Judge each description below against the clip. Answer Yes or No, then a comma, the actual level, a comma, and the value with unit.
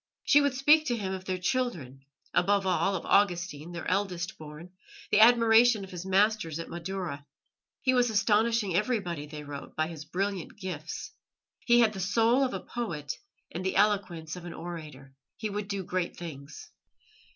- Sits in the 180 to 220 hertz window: Yes, high, 190 Hz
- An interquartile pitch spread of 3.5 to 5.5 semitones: Yes, average, 4.4 semitones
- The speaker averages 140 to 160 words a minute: No, average, 175 wpm